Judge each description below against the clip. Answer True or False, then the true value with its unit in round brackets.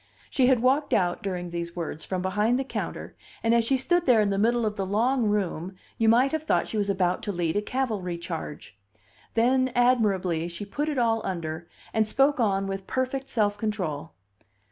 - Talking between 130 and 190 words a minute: False (200 wpm)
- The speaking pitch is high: True (210 Hz)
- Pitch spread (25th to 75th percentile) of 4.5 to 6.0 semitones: True (5.4 semitones)